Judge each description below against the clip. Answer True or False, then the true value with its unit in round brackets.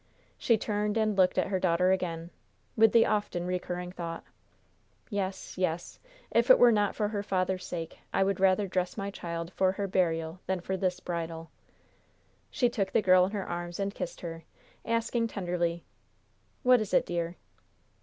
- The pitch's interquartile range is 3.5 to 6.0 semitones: False (2.9 semitones)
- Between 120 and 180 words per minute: True (175 wpm)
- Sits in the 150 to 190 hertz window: True (185 Hz)